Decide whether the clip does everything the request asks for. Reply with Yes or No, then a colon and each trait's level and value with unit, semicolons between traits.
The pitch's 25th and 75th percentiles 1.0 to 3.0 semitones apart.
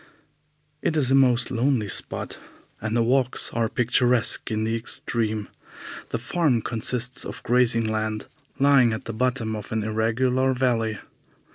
Yes: narrow, 2.5 semitones